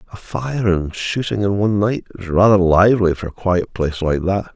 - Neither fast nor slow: No, fast, 210 wpm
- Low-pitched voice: Yes, very low, 95 Hz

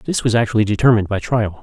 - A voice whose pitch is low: Yes, low, 110 Hz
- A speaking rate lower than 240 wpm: Yes, fast, 220 wpm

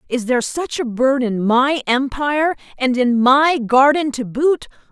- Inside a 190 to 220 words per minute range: No, average, 170 wpm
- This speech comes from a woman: Yes, female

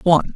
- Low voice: No, medium, 175 Hz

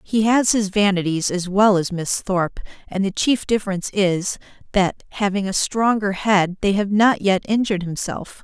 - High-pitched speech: Yes, high, 200 Hz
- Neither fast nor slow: Yes, average, 180 wpm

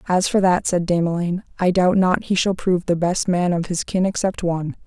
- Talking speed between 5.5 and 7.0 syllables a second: Yes, 5.6 syllables/s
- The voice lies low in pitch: No, medium, 180 Hz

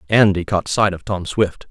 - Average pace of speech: No, fast, 210 wpm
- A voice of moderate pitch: No, very low, 95 Hz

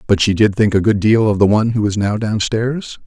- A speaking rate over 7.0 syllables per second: No, 5.6 syllables/s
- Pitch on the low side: Yes, low, 105 Hz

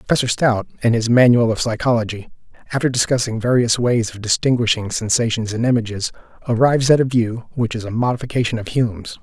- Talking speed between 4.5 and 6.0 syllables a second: No, 6.2 syllables/s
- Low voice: Yes, low, 115 Hz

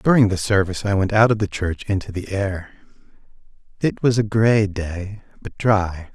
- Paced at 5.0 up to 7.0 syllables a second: No, 4.8 syllables/s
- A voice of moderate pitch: No, low, 100 Hz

